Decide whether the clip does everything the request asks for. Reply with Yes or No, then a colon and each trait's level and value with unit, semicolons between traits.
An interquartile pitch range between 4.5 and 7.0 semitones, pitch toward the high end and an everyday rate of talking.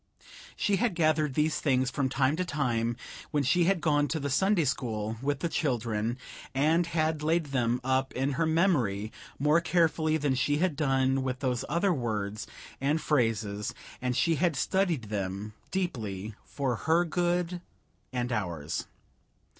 No: average, 5.1 semitones; medium, 140 Hz; average, 155 wpm